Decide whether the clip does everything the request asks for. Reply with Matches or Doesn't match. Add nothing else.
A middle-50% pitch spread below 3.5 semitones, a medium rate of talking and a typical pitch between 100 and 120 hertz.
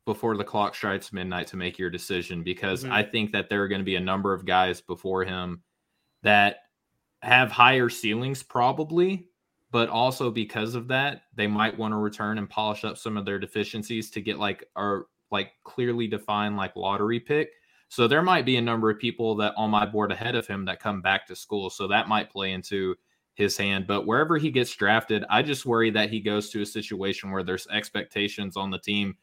Doesn't match